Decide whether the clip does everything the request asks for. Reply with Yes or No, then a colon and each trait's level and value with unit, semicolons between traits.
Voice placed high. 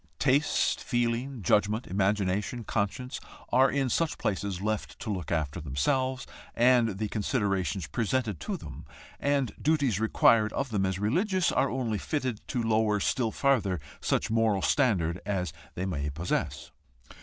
No: low, 110 Hz